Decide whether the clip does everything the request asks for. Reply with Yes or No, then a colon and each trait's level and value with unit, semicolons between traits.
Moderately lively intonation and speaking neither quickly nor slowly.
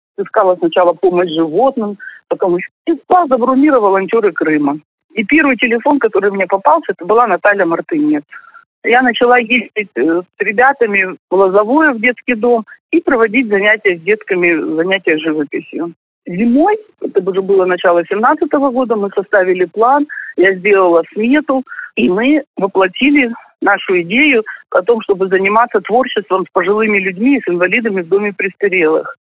No: wide, 6.1 semitones; average, 140 wpm